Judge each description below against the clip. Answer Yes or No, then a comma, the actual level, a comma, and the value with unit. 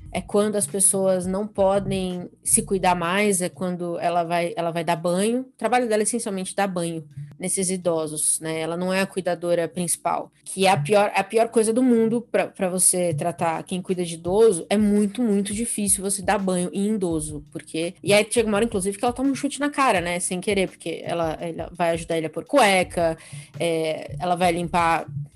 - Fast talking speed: Yes, fast, 210 wpm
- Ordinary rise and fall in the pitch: Yes, average, 3.4 semitones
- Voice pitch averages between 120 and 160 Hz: No, medium, 185 Hz